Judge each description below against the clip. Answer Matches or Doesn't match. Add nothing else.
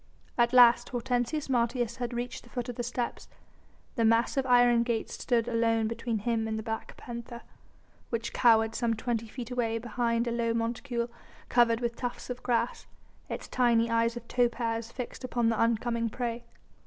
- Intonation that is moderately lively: Doesn't match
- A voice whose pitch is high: Matches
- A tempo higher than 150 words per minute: Matches